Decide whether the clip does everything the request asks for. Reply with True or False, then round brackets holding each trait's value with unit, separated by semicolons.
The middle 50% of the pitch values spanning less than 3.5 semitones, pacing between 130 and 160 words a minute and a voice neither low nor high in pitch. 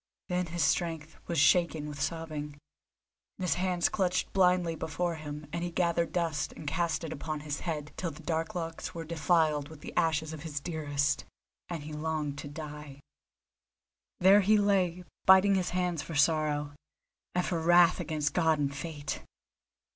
False (2.7 semitones; 170 wpm; 160 Hz)